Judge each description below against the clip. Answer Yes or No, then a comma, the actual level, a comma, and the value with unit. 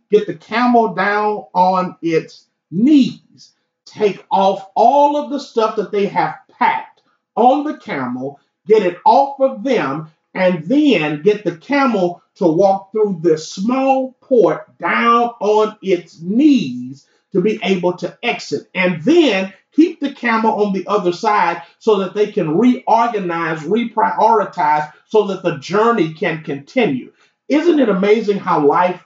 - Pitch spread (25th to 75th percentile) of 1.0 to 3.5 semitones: No, average, 5.1 semitones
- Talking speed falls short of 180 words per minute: Yes, average, 145 wpm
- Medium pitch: No, high, 210 Hz